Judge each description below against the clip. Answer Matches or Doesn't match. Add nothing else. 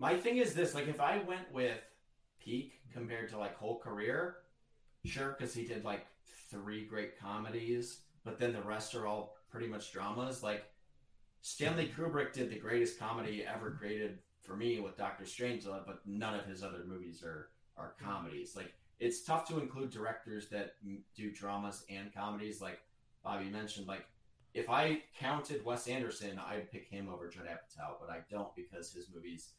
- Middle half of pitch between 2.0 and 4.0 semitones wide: Matches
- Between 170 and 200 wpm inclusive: Matches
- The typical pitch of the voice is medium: Doesn't match